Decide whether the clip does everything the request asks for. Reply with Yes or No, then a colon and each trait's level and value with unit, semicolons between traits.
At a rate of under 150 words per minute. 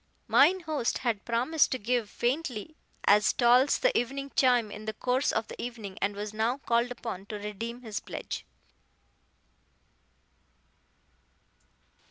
Yes: slow, 135 wpm